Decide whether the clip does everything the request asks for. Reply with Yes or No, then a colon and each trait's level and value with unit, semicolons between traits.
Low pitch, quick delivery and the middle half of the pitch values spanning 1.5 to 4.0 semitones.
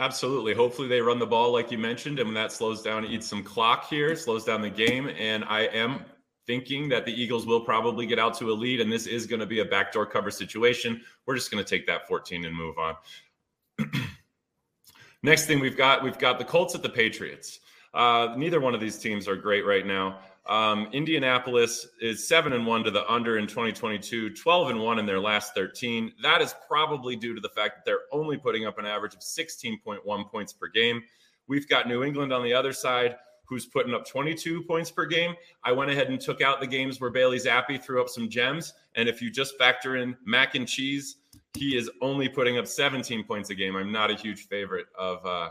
Yes: low, 120 Hz; fast, 225 wpm; average, 3.7 semitones